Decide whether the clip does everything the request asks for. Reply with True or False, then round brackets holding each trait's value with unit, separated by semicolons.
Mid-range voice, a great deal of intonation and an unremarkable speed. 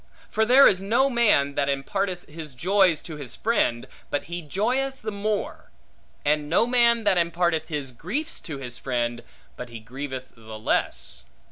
True (165 Hz; 7.8 semitones; 165 wpm)